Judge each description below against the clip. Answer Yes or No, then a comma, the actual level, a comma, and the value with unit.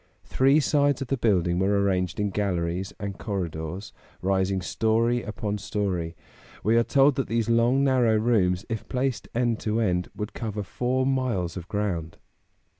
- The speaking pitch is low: Yes, low, 105 Hz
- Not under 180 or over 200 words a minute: No, average, 160 wpm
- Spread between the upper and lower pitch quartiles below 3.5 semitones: No, average, 4.4 semitones